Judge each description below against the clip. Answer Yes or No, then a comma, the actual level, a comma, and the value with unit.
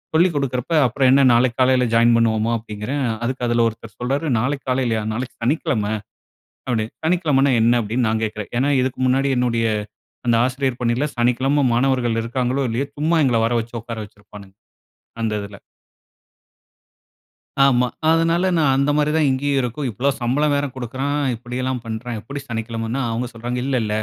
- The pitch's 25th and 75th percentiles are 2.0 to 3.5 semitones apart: Yes, average, 3.2 semitones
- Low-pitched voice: Yes, low, 125 Hz